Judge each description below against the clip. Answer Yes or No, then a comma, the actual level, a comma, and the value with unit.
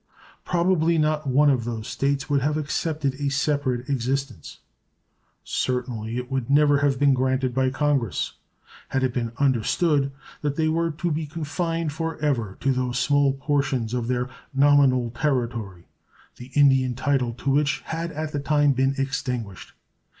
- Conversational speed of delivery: Yes, average, 155 wpm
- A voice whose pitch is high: No, medium, 140 Hz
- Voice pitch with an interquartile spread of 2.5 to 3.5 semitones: Yes, average, 2.9 semitones